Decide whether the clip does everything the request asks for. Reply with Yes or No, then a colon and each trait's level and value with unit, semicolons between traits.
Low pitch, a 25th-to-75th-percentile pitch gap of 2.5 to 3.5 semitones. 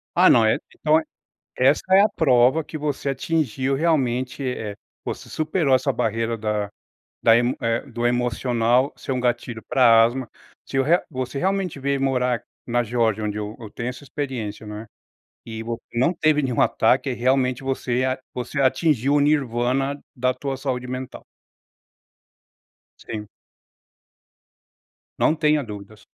Yes: low, 125 Hz; average, 2.9 semitones